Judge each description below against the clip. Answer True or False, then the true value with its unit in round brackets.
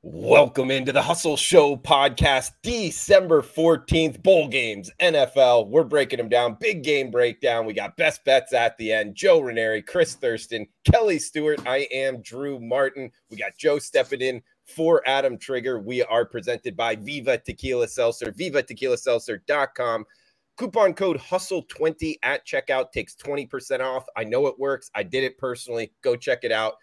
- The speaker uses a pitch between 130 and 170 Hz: True (140 Hz)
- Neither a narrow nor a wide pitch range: False (6.4 semitones)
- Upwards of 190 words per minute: False (165 wpm)